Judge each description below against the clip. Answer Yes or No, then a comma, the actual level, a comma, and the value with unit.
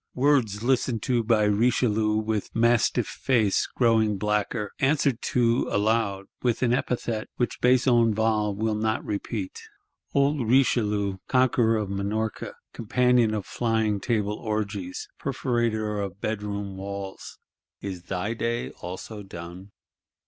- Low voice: Yes, low, 110 Hz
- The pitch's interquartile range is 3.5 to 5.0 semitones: No, average, 2.7 semitones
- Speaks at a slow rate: Yes, slow, 115 wpm